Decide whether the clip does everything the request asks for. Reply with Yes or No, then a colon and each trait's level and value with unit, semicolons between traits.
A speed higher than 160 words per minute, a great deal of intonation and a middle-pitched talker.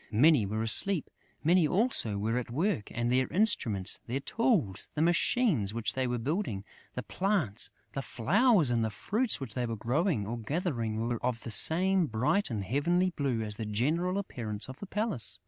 No: average, 180 wpm; wide, 8.2 semitones; low, 130 Hz